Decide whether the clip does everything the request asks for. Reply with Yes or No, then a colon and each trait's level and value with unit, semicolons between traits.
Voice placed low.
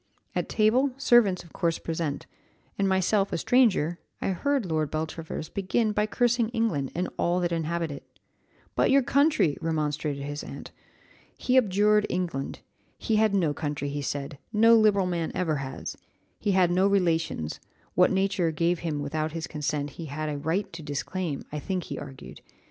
No: medium, 170 Hz